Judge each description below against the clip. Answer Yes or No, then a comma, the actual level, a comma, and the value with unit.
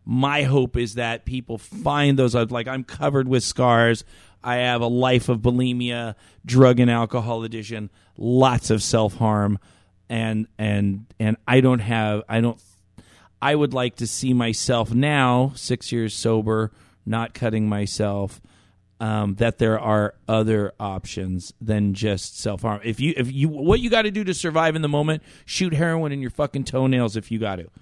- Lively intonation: No, average, 3.1 semitones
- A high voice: No, low, 115 Hz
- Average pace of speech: Yes, average, 175 wpm